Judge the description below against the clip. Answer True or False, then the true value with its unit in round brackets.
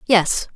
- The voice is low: False (200 Hz)